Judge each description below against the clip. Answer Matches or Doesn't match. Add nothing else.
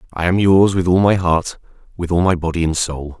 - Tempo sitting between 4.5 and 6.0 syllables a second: Matches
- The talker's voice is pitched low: Matches